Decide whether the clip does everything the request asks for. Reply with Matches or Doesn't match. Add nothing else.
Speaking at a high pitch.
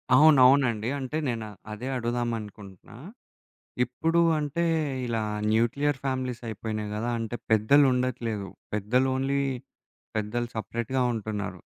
Doesn't match